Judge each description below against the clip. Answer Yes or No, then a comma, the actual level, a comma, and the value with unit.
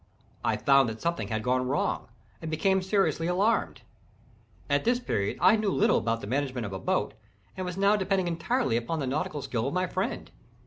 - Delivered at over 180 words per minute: Yes, average, 195 wpm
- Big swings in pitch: Yes, wide, 7.2 semitones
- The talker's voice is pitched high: No, medium, 165 Hz